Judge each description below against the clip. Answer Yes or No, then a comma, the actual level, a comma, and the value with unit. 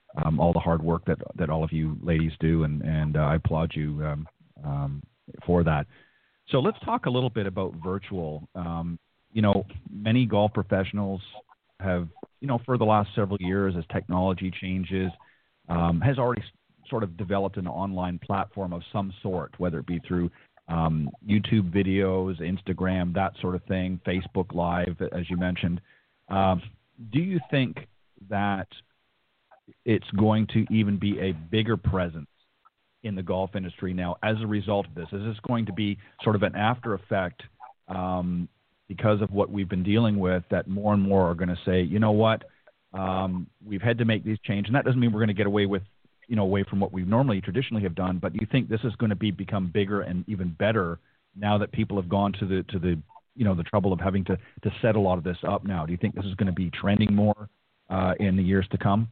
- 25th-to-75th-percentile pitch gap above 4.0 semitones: No, average, 2.8 semitones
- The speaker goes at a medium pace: No, fast, 215 wpm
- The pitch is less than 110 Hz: Yes, very low, 95 Hz